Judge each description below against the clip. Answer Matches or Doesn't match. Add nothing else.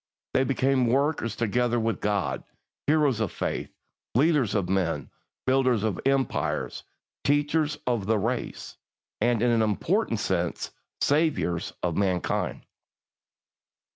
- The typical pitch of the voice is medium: Doesn't match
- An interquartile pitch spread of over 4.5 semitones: Matches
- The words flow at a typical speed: Doesn't match